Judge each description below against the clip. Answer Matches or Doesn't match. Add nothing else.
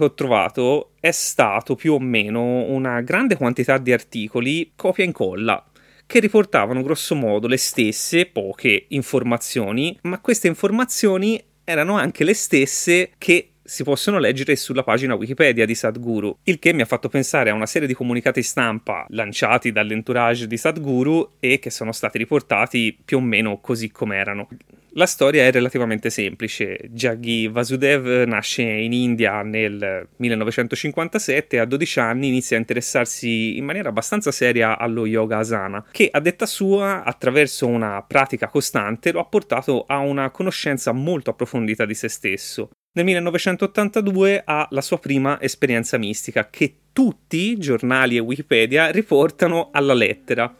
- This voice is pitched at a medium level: Doesn't match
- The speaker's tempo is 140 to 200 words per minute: Matches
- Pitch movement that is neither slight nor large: Doesn't match